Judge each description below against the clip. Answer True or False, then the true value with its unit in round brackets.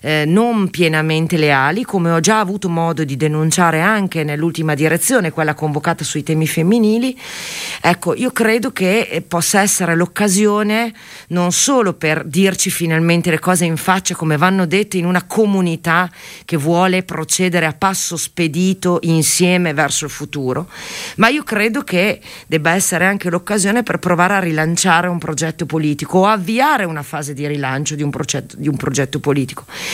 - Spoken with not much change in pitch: False (3.3 semitones)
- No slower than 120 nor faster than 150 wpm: False (160 wpm)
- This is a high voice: False (170 Hz)